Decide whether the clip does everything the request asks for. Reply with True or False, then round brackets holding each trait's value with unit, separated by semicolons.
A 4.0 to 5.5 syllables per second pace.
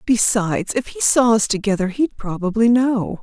True (4.9 syllables/s)